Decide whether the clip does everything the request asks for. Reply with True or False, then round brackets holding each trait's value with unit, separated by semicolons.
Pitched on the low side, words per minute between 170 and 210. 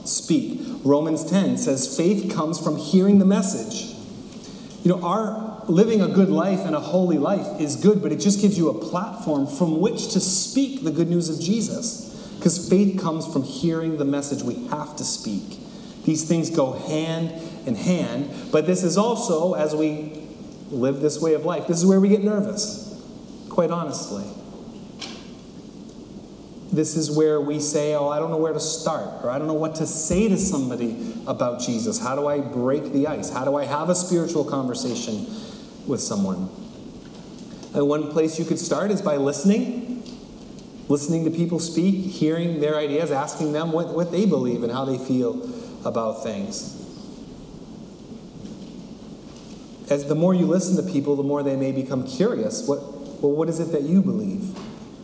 False (175 Hz; 175 wpm)